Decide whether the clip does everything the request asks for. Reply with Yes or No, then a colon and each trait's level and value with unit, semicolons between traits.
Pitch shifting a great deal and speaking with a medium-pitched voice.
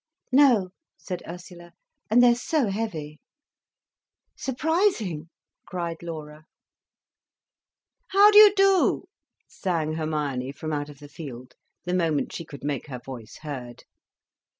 Yes: wide, 7.6 semitones; medium, 165 Hz